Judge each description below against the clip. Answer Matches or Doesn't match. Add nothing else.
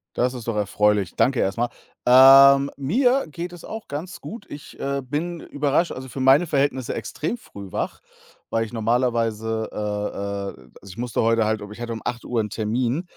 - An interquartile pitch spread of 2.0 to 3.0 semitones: Doesn't match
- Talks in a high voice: Doesn't match